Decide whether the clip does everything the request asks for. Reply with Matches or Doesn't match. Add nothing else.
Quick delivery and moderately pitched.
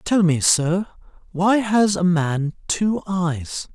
Doesn't match